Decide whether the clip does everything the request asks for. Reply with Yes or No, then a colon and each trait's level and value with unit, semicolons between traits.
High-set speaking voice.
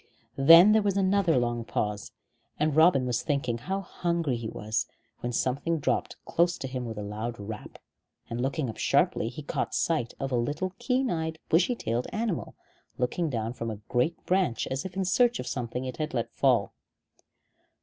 No: low, 135 Hz